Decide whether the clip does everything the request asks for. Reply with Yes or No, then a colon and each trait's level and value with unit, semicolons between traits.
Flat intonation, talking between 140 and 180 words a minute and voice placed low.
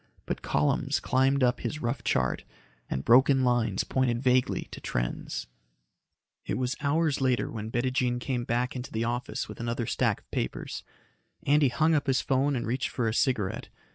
Yes: narrow, 2.2 semitones; average, 170 wpm; low, 125 Hz